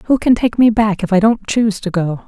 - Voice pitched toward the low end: No, high, 210 Hz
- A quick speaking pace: Yes, fast, 290 wpm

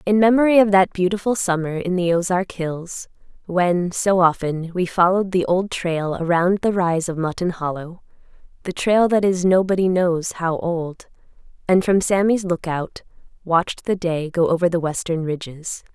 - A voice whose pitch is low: No, medium, 180 Hz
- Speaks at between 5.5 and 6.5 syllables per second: No, 4.7 syllables/s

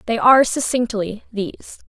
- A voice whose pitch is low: No, high, 225 Hz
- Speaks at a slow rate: Yes, slow, 125 wpm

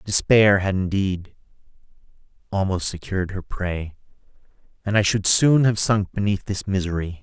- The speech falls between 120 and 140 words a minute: Yes, slow, 135 wpm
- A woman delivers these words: No, male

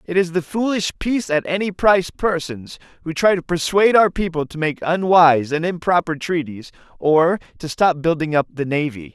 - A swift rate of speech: No, average, 185 wpm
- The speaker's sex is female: No, male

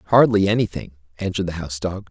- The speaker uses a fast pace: No, average, 170 wpm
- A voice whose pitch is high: No, very low, 95 Hz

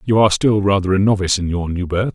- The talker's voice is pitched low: Yes, low, 100 Hz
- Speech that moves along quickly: Yes, fast, 280 wpm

